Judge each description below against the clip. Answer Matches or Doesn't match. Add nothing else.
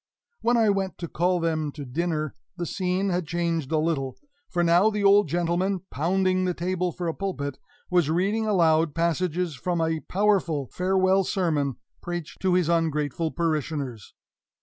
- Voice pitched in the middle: Matches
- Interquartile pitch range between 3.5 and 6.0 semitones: Doesn't match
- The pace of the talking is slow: Doesn't match